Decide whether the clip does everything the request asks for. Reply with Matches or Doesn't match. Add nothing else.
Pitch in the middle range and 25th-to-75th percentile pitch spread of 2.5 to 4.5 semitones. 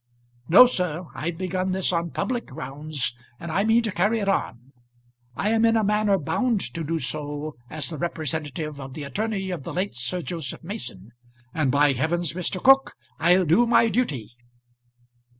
Doesn't match